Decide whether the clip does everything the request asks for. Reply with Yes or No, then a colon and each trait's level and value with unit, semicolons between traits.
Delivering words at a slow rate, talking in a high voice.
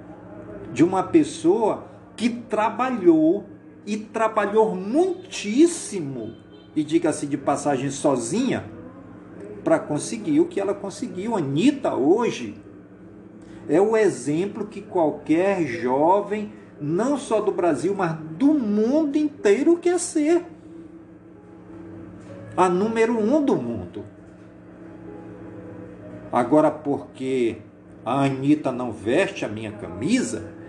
Yes: slow, 100 wpm; high, 205 Hz